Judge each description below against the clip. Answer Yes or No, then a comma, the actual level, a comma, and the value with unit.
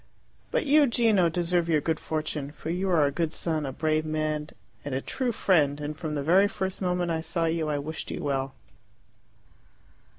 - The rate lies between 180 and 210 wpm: Yes, average, 195 wpm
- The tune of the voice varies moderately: Yes, average, 3.0 semitones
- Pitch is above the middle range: No, medium, 160 Hz